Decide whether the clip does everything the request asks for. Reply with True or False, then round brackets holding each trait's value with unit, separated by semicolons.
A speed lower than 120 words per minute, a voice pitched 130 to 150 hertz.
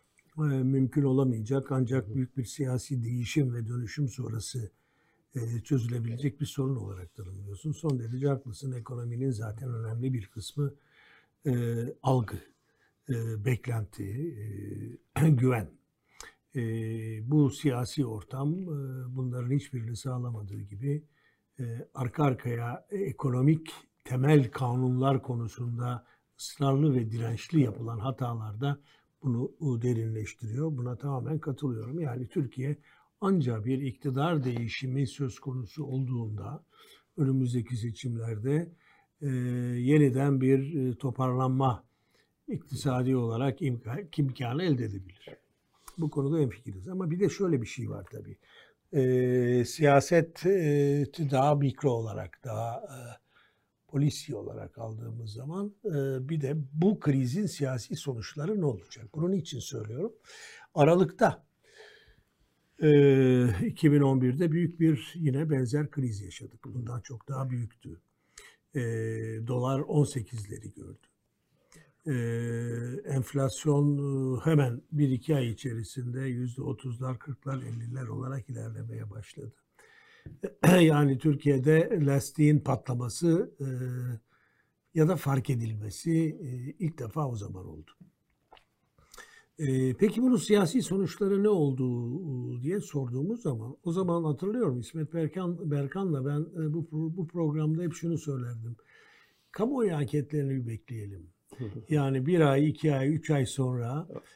True (105 wpm; 135 Hz)